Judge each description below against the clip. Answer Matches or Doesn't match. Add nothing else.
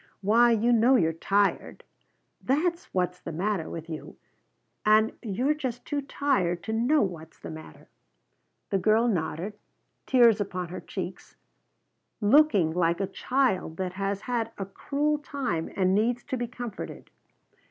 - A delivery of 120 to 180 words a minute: Matches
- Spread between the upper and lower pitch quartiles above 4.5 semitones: Matches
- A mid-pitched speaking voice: Doesn't match